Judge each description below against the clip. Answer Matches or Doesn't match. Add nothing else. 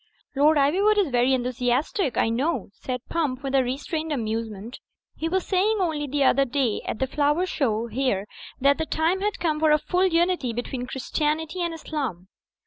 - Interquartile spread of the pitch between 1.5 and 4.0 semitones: Doesn't match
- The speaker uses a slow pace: Doesn't match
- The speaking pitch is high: Matches